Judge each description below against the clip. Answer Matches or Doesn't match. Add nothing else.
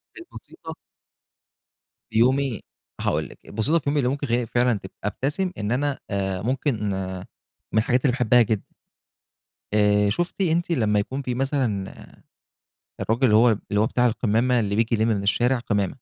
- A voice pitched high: Doesn't match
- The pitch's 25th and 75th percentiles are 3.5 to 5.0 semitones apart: Matches